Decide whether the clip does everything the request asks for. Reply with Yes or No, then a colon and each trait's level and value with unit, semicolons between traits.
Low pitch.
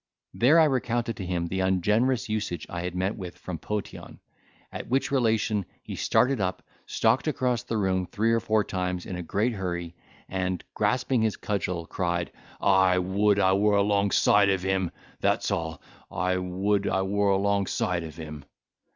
Yes: very low, 95 Hz